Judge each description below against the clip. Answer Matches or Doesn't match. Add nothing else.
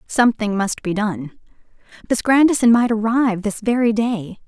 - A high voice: Matches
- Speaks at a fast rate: Doesn't match